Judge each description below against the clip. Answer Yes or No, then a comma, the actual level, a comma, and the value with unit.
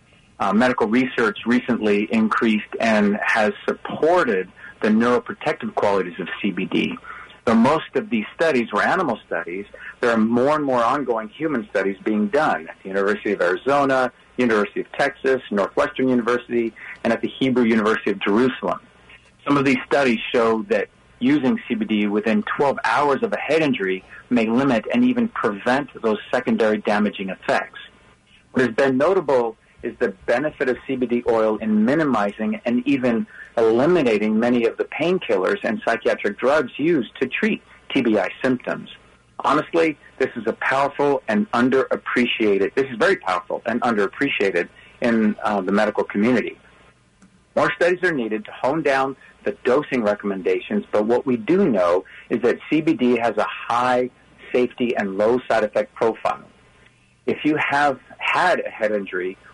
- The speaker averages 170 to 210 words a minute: No, average, 150 wpm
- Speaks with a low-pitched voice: Yes, low, 125 Hz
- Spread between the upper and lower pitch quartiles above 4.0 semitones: Yes, average, 4.5 semitones